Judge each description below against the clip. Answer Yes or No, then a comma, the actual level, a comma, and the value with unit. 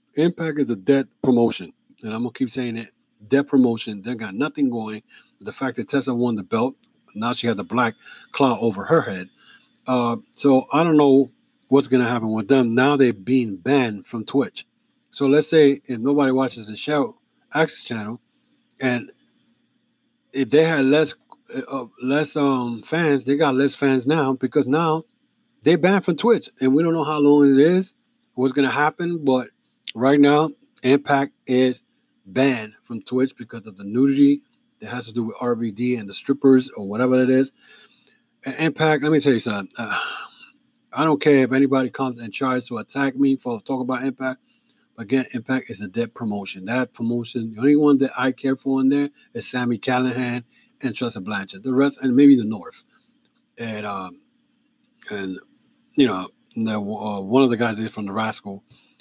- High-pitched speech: No, low, 135 Hz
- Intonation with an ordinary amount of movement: Yes, average, 4.0 semitones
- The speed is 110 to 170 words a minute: No, average, 185 wpm